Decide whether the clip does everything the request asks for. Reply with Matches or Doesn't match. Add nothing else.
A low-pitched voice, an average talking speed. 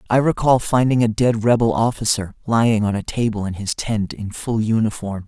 Matches